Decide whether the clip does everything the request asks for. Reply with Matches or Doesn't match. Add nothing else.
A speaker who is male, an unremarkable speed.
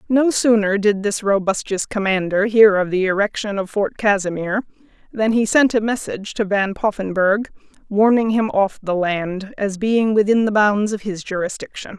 Doesn't match